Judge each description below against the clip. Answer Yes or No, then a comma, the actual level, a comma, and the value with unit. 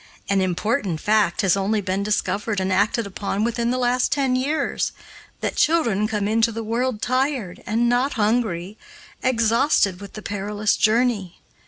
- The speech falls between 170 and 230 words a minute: No, average, 155 wpm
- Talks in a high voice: Yes, high, 215 Hz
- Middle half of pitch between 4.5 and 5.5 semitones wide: No, average, 3.4 semitones